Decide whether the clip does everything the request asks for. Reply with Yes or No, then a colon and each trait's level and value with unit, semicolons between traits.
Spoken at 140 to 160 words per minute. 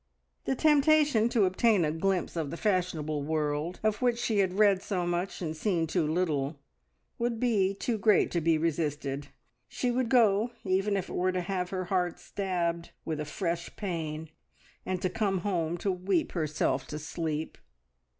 No: average, 175 wpm